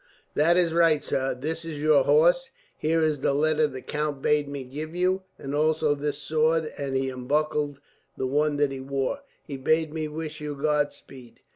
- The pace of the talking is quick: No, average, 190 wpm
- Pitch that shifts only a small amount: Yes, narrow, 2.1 semitones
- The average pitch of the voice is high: No, medium, 150 Hz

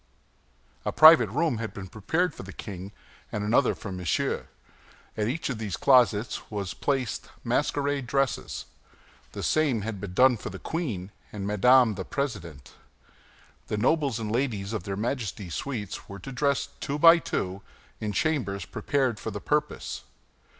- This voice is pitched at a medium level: No, low, 115 Hz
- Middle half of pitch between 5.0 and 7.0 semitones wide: Yes, wide, 5.6 semitones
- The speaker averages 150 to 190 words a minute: Yes, average, 155 wpm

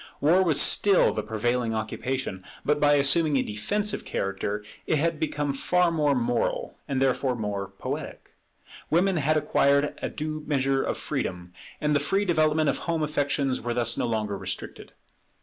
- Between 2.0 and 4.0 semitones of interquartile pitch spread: No, average, 4.9 semitones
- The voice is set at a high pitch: No, medium, 140 Hz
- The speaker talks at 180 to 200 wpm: No, average, 165 wpm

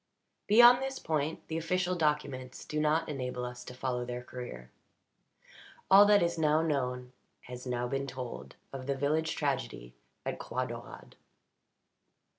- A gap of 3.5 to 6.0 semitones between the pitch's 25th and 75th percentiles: Yes, average, 4.4 semitones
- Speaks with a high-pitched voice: No, medium, 140 Hz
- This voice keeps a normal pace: Yes, average, 145 wpm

